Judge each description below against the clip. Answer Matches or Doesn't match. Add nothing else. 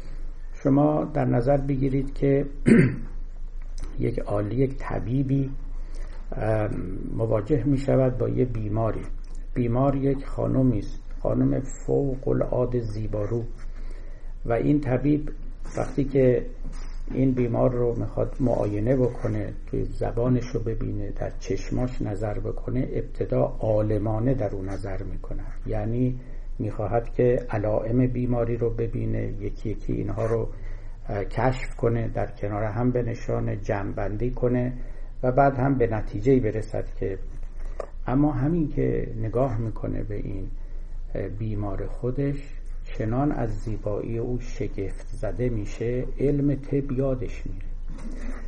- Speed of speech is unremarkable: Matches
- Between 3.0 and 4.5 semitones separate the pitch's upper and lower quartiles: Matches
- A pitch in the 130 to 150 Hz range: Doesn't match